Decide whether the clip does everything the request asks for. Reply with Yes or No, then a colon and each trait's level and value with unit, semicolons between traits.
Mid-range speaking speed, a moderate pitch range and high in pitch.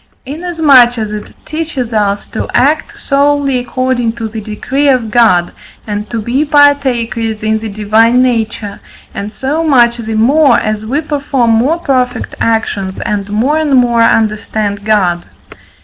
Yes: average, 150 wpm; average, 4.3 semitones; high, 235 Hz